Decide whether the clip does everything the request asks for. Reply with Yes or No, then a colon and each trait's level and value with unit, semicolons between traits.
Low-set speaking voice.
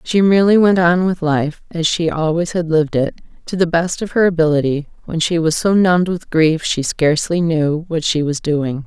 No: medium, 165 Hz